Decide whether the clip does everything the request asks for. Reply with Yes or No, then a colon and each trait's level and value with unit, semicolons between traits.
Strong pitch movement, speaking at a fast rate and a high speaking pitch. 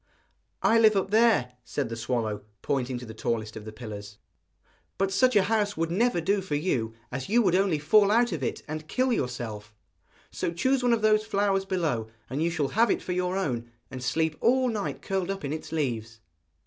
No: wide, 8.9 semitones; fast, 210 wpm; medium, 165 Hz